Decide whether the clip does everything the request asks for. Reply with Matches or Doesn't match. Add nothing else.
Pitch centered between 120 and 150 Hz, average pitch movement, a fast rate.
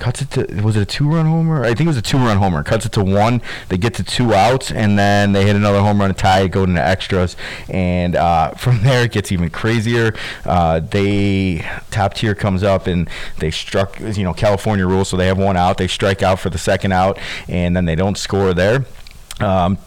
Doesn't match